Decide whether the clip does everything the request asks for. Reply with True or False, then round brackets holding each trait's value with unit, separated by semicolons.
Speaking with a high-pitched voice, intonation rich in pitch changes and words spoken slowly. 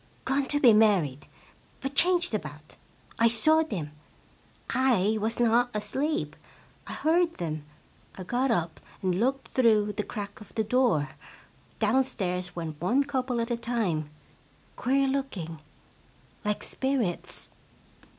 True (225 Hz; 6.5 semitones; 130 wpm)